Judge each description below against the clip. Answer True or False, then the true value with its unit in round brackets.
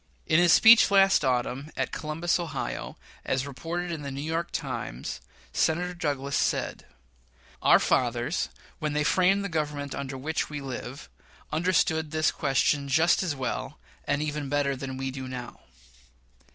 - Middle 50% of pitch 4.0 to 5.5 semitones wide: False (3.5 semitones)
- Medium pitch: True (150 Hz)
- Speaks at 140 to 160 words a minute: True (150 wpm)